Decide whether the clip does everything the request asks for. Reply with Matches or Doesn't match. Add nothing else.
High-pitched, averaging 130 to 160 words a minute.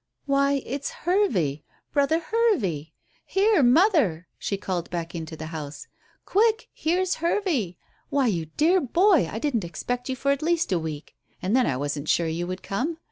Doesn't match